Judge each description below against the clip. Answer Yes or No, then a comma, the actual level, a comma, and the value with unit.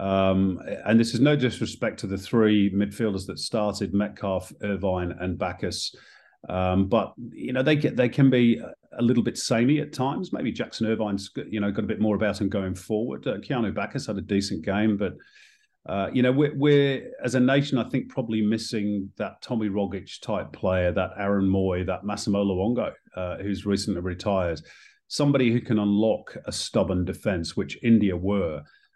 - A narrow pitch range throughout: No, average, 3.7 semitones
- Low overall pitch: Yes, low, 105 Hz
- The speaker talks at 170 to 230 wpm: Yes, average, 185 wpm